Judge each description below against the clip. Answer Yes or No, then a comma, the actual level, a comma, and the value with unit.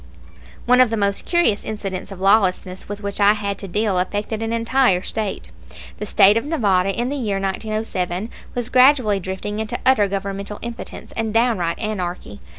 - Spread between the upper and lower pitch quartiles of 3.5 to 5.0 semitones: No, average, 2.8 semitones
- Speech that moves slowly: No, average, 170 wpm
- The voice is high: Yes, high, 210 Hz